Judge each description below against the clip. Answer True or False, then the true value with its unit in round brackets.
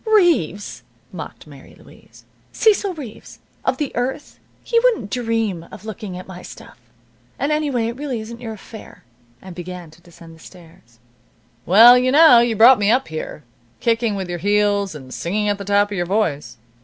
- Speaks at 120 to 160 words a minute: False (180 wpm)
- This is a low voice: False (210 Hz)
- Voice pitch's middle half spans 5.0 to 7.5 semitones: True (5.4 semitones)